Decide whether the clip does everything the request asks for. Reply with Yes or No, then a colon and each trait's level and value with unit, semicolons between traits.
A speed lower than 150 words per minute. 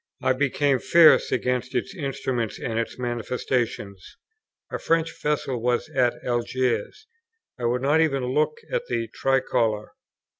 Yes: slow, 135 wpm